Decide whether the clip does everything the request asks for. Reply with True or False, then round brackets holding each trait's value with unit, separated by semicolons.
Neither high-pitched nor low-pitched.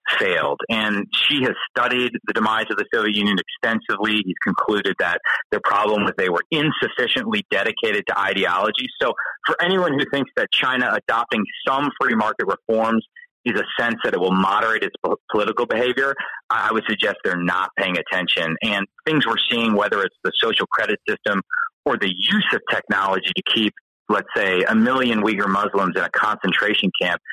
False (125 Hz)